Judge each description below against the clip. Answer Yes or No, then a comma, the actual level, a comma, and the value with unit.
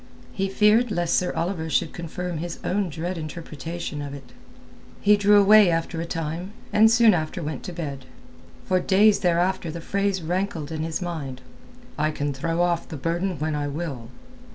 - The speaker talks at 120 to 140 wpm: No, average, 175 wpm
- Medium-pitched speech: Yes, medium, 170 Hz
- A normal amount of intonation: Yes, average, 3.5 semitones